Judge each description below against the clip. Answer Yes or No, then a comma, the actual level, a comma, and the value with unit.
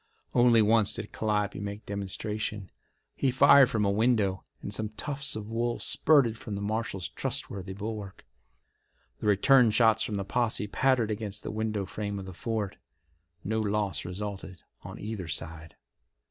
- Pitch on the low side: Yes, low, 105 Hz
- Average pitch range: No, narrow, 2.3 semitones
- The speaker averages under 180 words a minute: Yes, average, 155 wpm